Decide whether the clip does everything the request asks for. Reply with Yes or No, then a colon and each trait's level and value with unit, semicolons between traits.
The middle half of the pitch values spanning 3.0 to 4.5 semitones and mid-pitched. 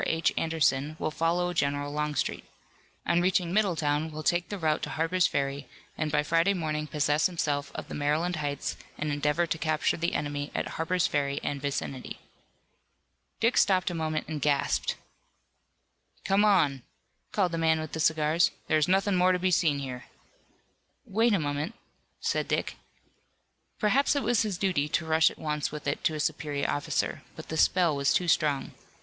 Yes: average, 3.4 semitones; medium, 155 Hz